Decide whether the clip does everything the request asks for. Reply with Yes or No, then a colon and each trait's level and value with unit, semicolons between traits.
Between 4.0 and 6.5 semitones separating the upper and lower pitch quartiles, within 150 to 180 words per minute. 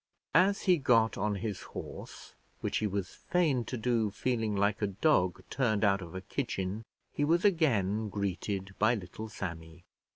Yes: average, 4.4 semitones; average, 165 wpm